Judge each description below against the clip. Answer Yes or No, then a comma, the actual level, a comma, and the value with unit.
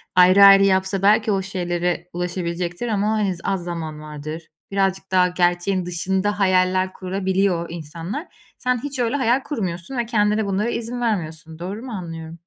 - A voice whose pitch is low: No, high, 190 Hz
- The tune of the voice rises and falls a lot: No, average, 3.0 semitones